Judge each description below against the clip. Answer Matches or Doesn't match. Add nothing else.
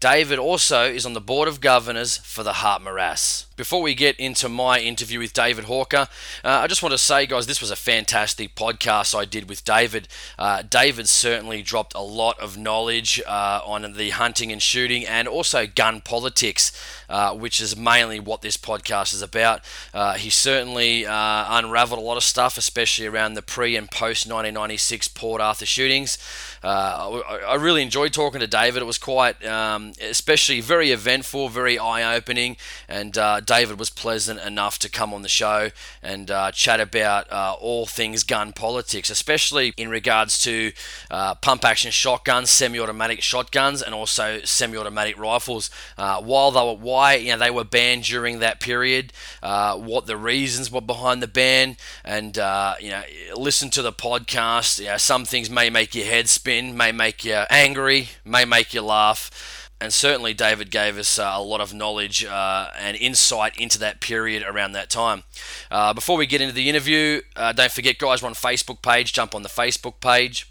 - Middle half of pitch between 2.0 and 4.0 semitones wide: Matches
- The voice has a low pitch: Matches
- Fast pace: Doesn't match